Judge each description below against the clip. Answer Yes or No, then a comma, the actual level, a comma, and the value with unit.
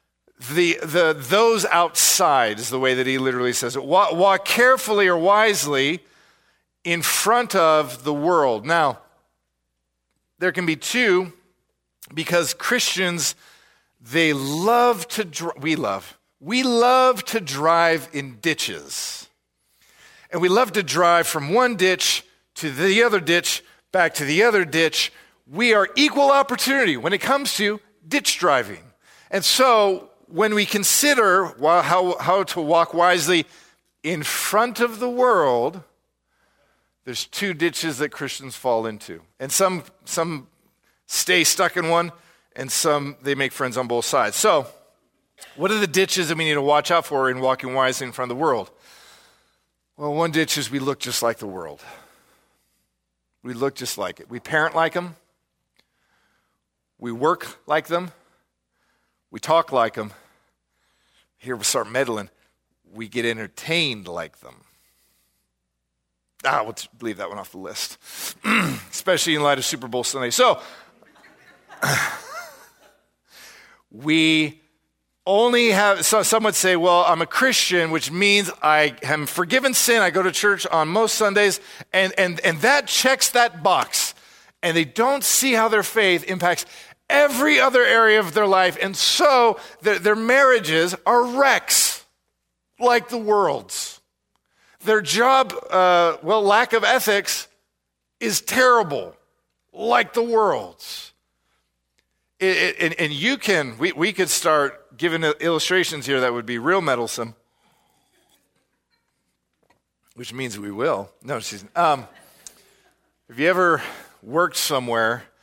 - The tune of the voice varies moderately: No, wide, 7.5 semitones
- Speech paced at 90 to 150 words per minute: Yes, average, 145 wpm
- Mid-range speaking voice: Yes, medium, 170 Hz